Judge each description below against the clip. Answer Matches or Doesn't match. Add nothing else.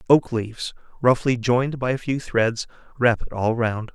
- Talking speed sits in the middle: Matches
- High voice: Doesn't match